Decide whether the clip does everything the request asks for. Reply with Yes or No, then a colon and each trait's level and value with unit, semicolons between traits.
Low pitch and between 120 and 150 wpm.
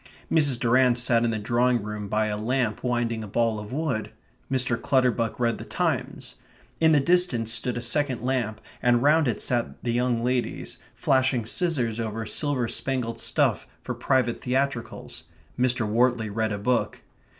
No: low, 120 Hz; average, 165 wpm